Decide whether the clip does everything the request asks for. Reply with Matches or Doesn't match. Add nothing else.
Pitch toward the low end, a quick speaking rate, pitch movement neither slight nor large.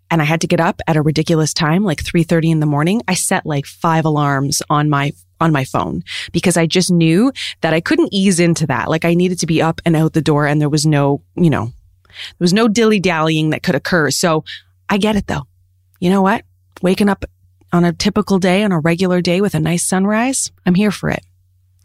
Doesn't match